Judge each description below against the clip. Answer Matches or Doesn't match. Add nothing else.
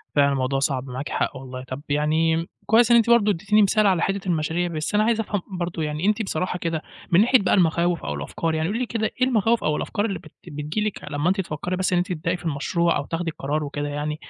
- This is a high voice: Doesn't match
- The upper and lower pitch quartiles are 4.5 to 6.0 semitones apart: Matches